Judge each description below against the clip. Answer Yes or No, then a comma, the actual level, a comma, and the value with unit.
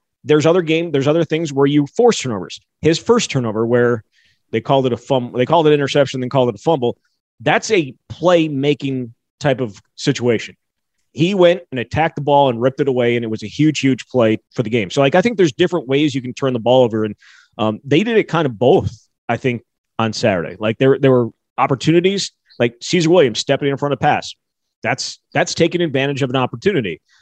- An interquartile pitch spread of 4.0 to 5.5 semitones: Yes, average, 4.3 semitones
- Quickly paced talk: Yes, fast, 225 wpm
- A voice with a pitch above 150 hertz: No, low, 135 Hz